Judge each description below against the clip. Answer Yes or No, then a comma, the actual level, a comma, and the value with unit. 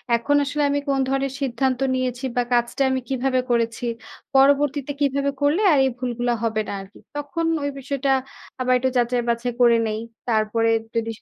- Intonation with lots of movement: No, average, 2.7 semitones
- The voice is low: No, very high, 255 Hz